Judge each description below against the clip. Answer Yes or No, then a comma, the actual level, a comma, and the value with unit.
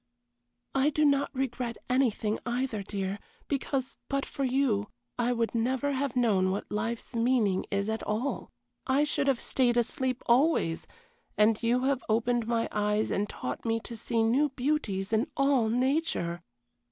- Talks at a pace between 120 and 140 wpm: No, average, 155 wpm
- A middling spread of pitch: Yes, average, 3.7 semitones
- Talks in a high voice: Yes, high, 240 Hz